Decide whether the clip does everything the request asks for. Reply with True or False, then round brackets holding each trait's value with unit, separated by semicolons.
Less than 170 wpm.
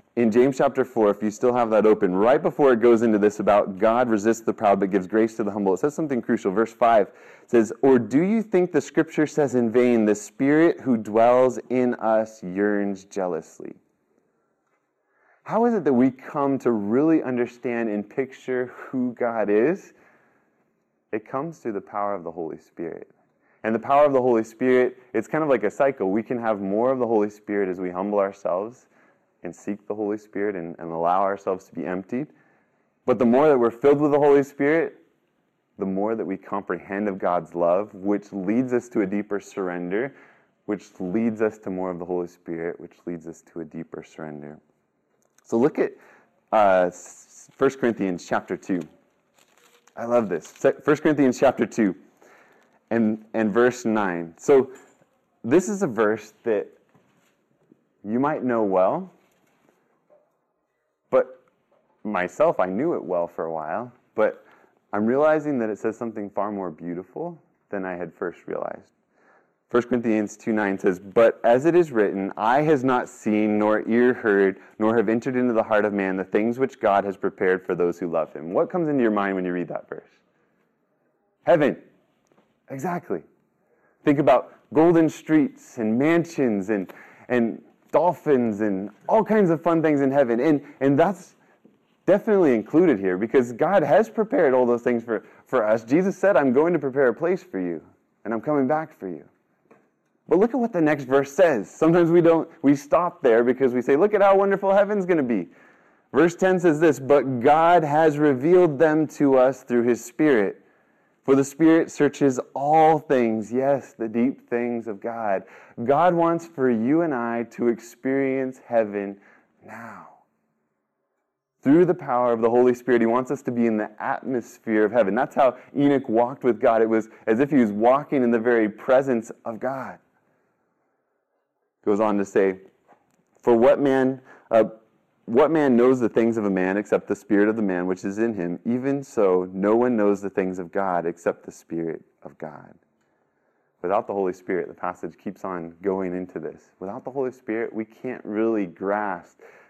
False (185 wpm)